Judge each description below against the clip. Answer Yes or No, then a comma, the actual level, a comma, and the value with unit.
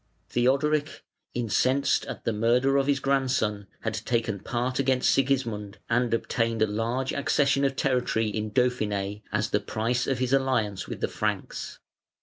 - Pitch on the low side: Yes, low, 120 Hz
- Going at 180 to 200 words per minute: No, average, 150 wpm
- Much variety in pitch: No, average, 3.6 semitones